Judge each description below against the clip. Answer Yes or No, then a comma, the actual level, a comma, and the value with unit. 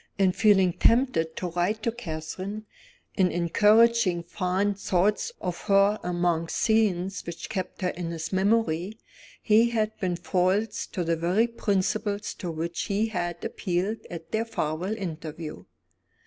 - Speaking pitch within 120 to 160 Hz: No, high, 190 Hz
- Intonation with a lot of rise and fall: No, average, 3.7 semitones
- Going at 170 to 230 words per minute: No, average, 140 wpm